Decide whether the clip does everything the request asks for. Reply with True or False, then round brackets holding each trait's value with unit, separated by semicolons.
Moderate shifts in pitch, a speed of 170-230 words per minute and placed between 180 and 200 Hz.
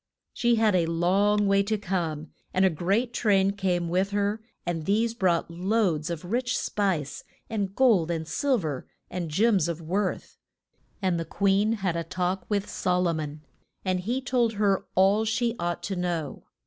True (3.5 semitones; 175 wpm; 190 Hz)